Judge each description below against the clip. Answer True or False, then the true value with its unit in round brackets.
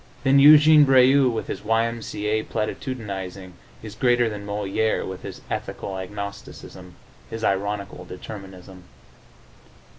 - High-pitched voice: False (105 Hz)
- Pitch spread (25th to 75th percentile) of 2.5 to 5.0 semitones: True (3.8 semitones)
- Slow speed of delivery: True (125 wpm)